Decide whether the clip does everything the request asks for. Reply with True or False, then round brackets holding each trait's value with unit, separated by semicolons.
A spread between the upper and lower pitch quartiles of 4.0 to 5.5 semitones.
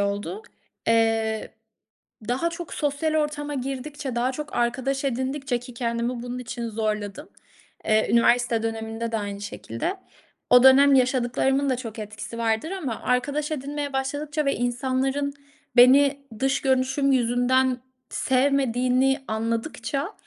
False (3.2 semitones)